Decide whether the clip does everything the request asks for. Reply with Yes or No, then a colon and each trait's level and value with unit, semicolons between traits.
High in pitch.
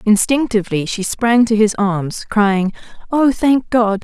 Yes: high, 220 Hz